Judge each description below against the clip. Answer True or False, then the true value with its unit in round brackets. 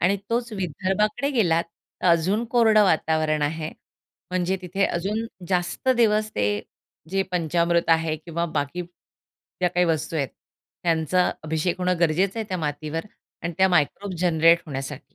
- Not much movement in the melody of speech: False (3.2 semitones)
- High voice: False (175 Hz)